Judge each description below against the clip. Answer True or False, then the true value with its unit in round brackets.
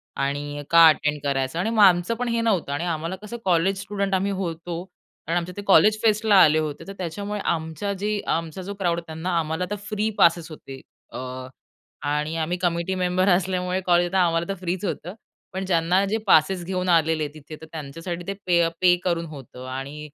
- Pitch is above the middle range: False (175 Hz)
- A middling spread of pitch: True (3.2 semitones)